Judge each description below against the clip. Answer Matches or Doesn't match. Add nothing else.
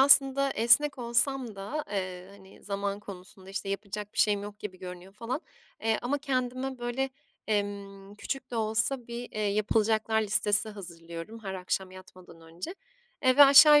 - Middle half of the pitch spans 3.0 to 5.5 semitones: Matches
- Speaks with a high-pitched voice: Matches